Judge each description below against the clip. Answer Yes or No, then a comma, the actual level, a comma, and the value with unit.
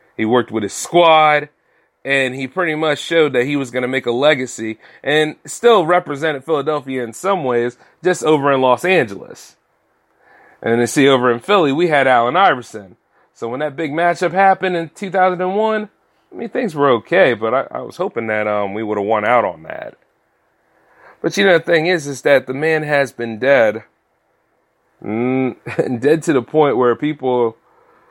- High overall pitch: No, medium, 140 Hz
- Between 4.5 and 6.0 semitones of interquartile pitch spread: Yes, average, 5.0 semitones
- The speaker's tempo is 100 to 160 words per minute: No, average, 190 wpm